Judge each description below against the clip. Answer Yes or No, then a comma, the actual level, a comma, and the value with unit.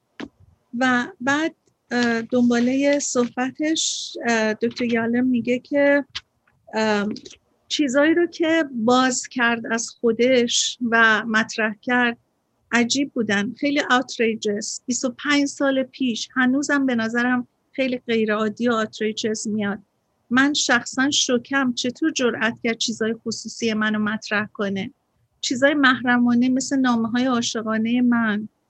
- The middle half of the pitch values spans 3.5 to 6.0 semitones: No, average, 2.8 semitones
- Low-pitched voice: No, high, 245 Hz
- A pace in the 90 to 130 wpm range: Yes, slow, 105 wpm